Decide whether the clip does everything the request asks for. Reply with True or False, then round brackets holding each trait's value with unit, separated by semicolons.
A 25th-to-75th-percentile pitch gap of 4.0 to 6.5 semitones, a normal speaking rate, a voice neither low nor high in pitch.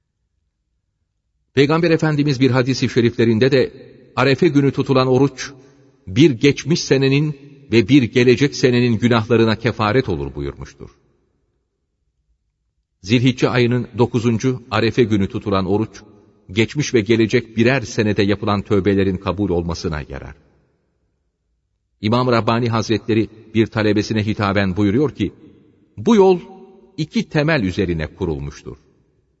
False (5.1 semitones; 105 wpm; 115 Hz)